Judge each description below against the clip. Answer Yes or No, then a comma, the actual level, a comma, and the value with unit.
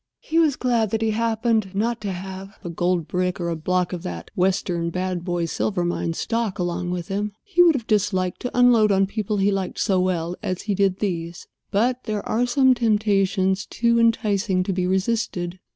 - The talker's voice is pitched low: No, high, 195 Hz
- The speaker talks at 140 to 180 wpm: No, average, 200 wpm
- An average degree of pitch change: Yes, average, 3.6 semitones